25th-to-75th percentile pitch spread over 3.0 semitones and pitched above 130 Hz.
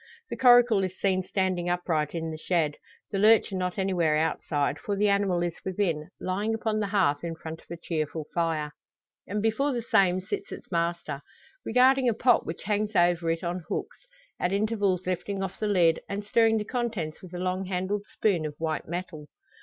Yes: average, 3.9 semitones; medium, 185 Hz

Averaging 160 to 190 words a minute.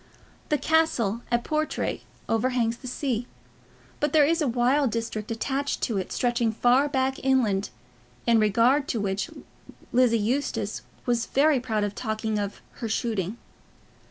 No: average, 145 wpm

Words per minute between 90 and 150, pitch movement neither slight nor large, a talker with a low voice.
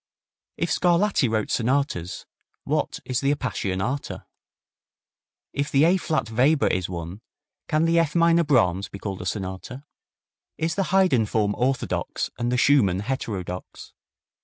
No: slow, 135 wpm; wide, 7.6 semitones; low, 125 Hz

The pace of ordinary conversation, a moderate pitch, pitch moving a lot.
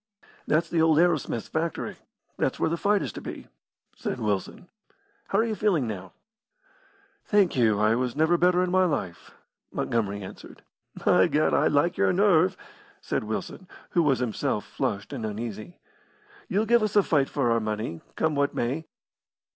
Yes: average, 170 wpm; medium, 150 Hz; wide, 7.9 semitones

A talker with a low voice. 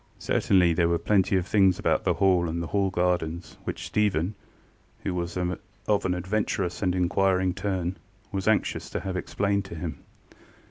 Yes: very low, 90 Hz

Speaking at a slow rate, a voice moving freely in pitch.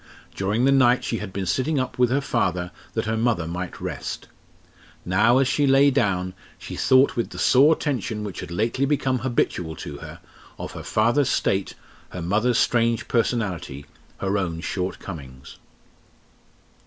No: average, 165 wpm; wide, 6.0 semitones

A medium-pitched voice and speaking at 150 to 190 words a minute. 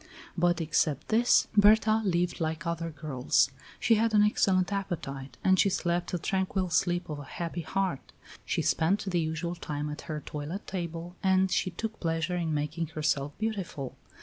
Yes: medium, 175 Hz; average, 170 wpm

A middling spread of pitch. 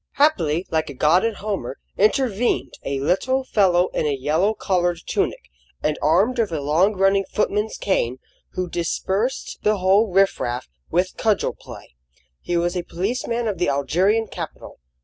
Yes: average, 4.7 semitones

